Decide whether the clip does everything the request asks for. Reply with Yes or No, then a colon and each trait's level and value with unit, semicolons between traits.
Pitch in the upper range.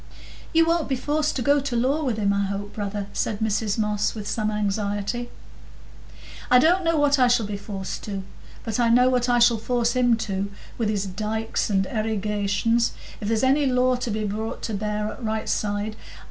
Yes: high, 220 Hz